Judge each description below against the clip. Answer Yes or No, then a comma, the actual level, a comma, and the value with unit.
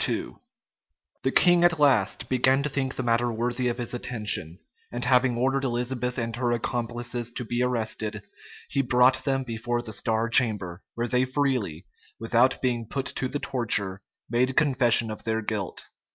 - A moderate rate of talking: Yes, average, 165 wpm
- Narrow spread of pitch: Yes, narrow, 2.3 semitones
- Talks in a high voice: No, low, 120 Hz